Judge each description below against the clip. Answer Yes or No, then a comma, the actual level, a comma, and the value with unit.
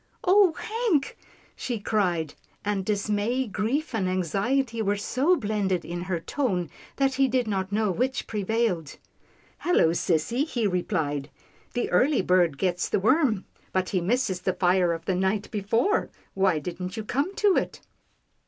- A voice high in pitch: Yes, high, 205 Hz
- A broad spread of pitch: Yes, wide, 5.7 semitones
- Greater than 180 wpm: No, average, 160 wpm